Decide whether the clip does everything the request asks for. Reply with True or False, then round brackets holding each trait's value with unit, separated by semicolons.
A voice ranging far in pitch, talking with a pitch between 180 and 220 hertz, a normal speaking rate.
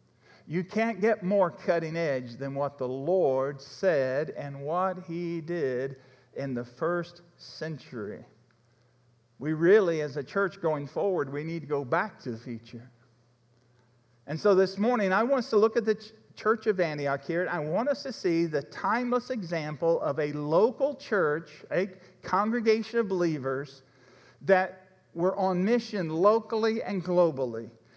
False (6.8 semitones; 165 Hz; 155 wpm)